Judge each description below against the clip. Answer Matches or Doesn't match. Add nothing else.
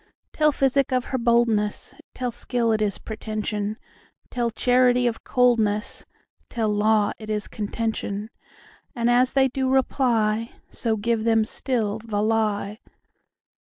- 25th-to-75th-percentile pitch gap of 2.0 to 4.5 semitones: Matches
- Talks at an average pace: Doesn't match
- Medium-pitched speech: Doesn't match